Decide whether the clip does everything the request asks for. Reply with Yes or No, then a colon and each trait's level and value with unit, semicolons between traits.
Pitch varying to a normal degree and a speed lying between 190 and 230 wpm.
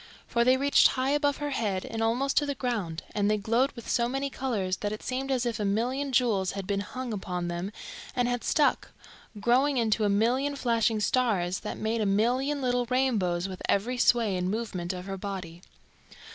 Yes: average, 4.5 semitones; average, 200 wpm